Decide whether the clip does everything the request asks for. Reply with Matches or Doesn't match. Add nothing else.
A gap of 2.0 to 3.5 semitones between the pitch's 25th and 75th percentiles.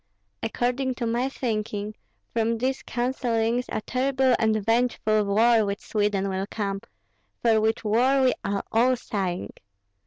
Matches